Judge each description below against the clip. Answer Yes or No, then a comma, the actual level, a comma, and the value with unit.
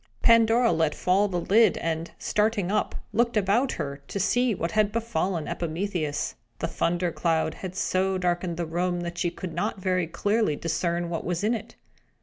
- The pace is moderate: Yes, average, 175 wpm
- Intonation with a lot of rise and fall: No, average, 3.8 semitones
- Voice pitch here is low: No, medium, 180 Hz